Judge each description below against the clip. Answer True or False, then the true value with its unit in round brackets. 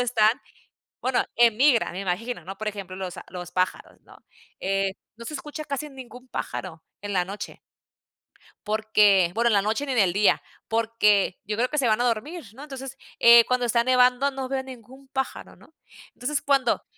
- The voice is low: False (235 Hz)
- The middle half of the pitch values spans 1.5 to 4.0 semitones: False (4.4 semitones)